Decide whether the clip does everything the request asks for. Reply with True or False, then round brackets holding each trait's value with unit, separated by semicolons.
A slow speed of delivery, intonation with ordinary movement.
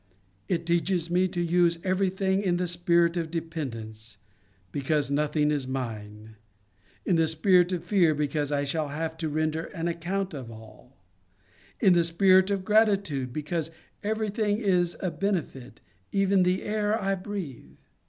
False (155 wpm; 4.2 semitones)